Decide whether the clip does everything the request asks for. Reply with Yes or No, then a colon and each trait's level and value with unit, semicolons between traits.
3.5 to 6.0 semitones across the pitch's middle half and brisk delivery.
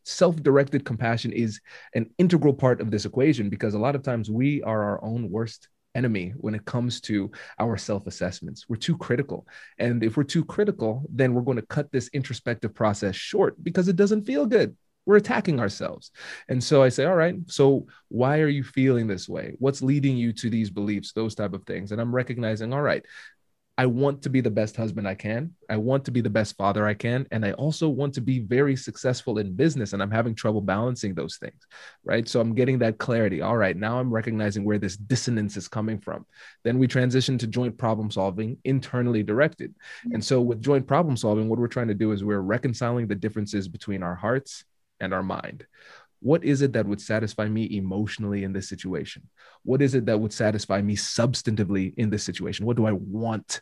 Yes: average, 3.8 semitones; fast, 215 wpm